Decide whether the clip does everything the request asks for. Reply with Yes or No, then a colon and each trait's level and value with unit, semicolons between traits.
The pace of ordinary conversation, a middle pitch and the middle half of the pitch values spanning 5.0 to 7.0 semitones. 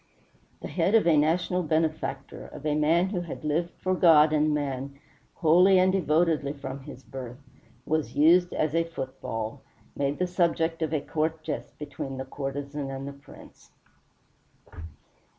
No: average, 155 wpm; medium, 155 Hz; average, 3.2 semitones